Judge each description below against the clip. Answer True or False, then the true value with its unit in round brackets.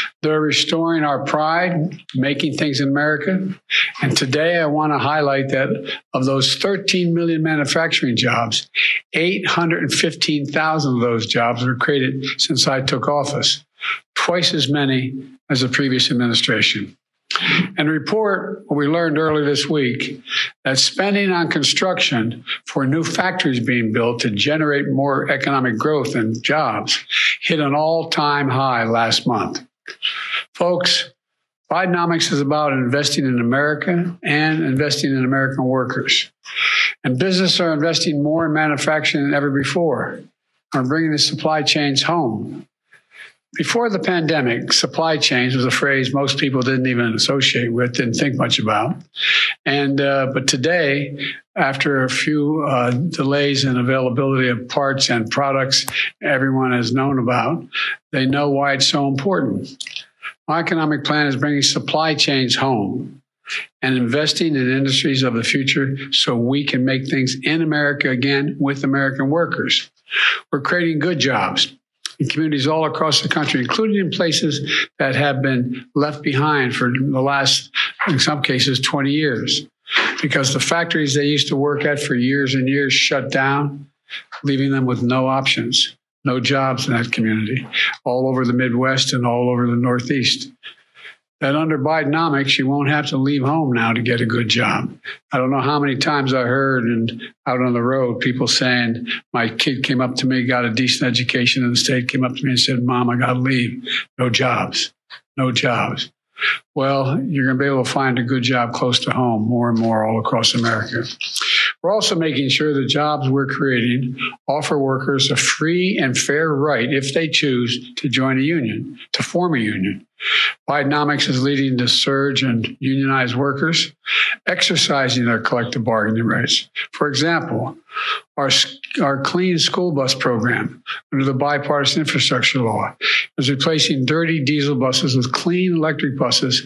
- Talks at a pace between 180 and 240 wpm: False (160 wpm)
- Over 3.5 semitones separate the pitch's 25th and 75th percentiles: False (3.0 semitones)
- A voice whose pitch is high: False (140 Hz)